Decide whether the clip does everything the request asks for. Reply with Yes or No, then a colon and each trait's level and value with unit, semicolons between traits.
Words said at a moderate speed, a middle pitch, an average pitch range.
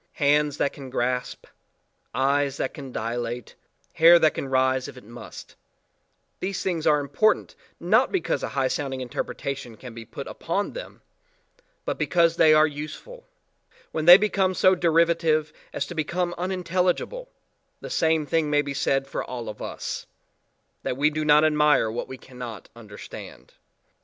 Yes: average, 155 wpm; medium, 150 Hz; average, 4.4 semitones